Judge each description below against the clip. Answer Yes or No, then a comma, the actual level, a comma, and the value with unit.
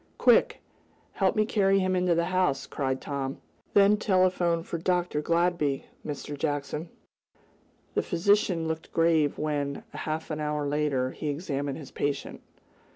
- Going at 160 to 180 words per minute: No, average, 140 wpm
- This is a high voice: No, medium, 160 Hz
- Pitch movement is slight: No, average, 3.8 semitones